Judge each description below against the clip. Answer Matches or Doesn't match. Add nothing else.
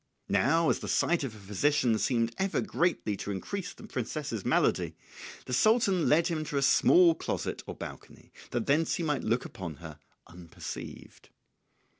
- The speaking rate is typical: Matches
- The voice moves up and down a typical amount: Doesn't match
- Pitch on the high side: Doesn't match